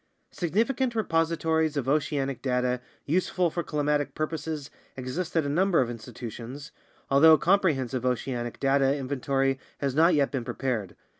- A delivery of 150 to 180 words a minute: No, average, 140 wpm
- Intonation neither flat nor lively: Yes, average, 4.0 semitones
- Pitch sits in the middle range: Yes, medium, 145 Hz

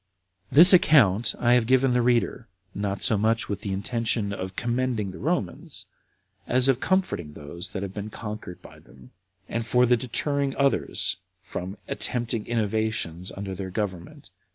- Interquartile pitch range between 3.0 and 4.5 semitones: Yes, average, 4.2 semitones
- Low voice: Yes, low, 110 Hz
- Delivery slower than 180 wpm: Yes, average, 160 wpm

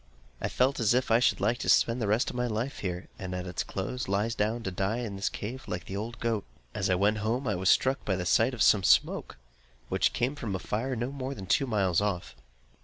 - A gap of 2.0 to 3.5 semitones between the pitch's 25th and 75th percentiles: No, average, 4.1 semitones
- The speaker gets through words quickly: Yes, fast, 250 wpm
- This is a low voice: Yes, low, 110 Hz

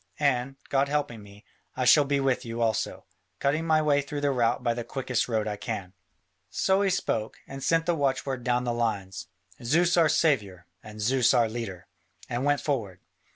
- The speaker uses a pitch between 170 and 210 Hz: No, low, 125 Hz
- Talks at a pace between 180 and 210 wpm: Yes, average, 190 wpm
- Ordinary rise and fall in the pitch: Yes, average, 4.2 semitones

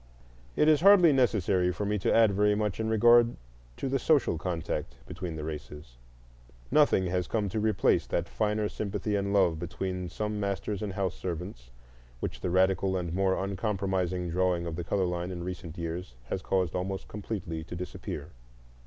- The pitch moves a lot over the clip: No, average, 3.2 semitones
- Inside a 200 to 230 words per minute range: No, average, 175 wpm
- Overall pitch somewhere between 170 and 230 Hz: No, very low, 95 Hz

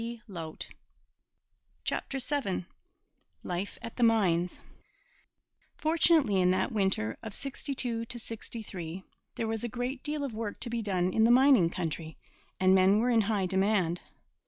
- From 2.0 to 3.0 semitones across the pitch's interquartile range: No, average, 4.7 semitones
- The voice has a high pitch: Yes, high, 220 Hz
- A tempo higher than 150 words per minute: No, slow, 135 wpm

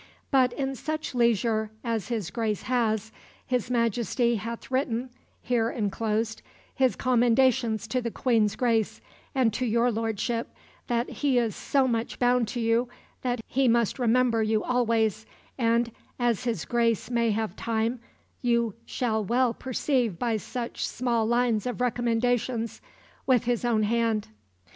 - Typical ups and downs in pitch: No, narrow, 1.9 semitones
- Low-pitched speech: No, high, 235 Hz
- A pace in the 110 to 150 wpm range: Yes, average, 145 wpm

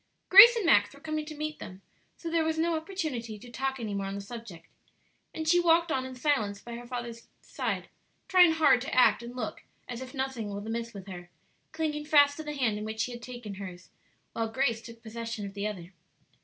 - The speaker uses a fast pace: Yes, fast, 225 wpm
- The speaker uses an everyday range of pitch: No, wide, 6.1 semitones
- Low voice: No, high, 240 Hz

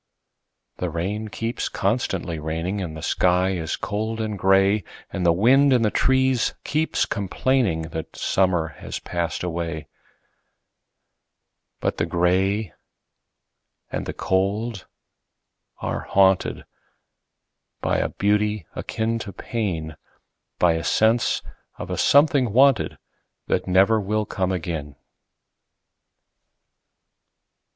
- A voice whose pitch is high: No, very low, 95 Hz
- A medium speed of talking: No, slow, 95 wpm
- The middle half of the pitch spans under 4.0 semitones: No, average, 4.3 semitones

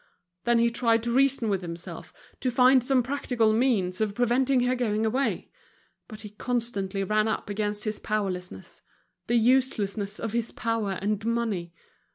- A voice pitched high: Yes, high, 225 Hz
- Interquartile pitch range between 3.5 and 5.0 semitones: No, average, 3.0 semitones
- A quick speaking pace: No, average, 160 wpm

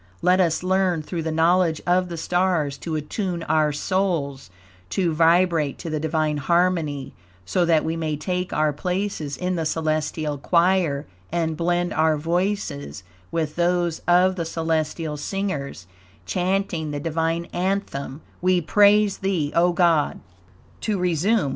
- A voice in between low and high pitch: Yes, medium, 165 Hz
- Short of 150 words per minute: Yes, average, 140 wpm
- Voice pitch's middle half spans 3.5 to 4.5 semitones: No, average, 2.9 semitones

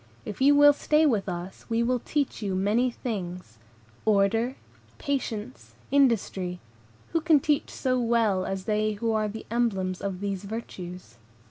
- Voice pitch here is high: Yes, high, 220 Hz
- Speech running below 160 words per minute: Yes, average, 150 wpm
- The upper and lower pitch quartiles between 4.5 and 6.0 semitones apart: Yes, average, 4.8 semitones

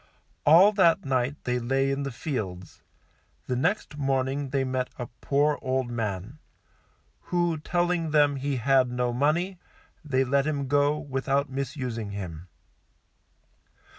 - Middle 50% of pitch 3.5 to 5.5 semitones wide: No, average, 3.0 semitones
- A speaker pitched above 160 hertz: No, low, 135 Hz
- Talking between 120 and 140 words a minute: Yes, slow, 135 wpm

